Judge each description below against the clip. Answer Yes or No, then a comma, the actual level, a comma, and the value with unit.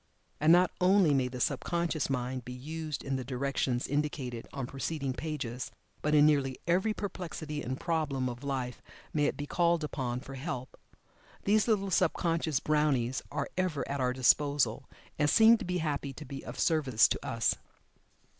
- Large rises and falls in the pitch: No, average, 4.0 semitones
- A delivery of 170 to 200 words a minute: Yes, average, 175 wpm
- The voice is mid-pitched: Yes, medium, 145 Hz